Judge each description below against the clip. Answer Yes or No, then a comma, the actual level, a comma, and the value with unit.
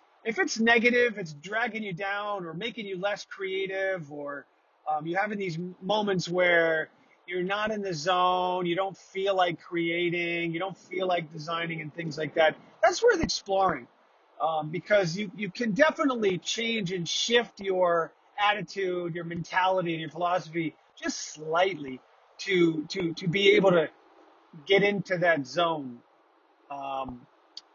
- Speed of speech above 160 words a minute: No, average, 150 wpm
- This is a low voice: No, medium, 180 Hz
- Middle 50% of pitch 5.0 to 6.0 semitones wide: No, average, 3.2 semitones